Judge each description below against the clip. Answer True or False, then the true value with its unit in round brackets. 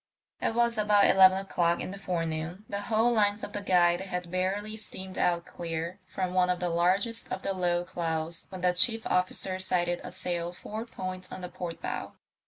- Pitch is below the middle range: False (185 Hz)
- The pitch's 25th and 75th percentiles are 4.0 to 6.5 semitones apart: False (2.4 semitones)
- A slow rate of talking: False (195 wpm)